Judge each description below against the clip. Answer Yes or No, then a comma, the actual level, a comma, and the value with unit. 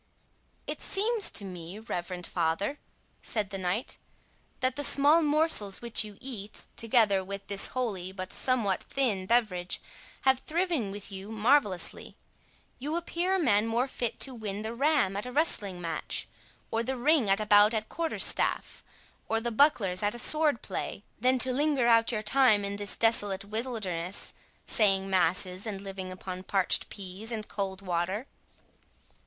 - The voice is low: No, high, 215 Hz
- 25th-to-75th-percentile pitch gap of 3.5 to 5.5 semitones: Yes, average, 4.8 semitones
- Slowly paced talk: No, average, 160 wpm